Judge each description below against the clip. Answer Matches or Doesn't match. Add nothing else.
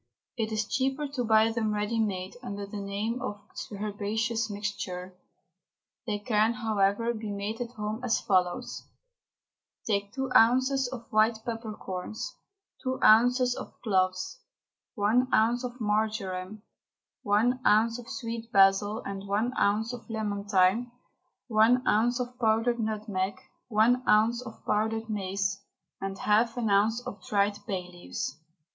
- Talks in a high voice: Matches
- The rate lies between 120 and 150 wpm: Matches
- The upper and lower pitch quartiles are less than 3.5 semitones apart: Matches